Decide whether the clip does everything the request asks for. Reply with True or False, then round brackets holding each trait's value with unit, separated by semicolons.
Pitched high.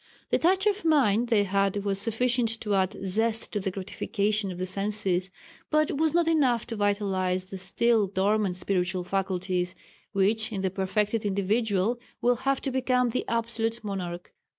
True (205 Hz)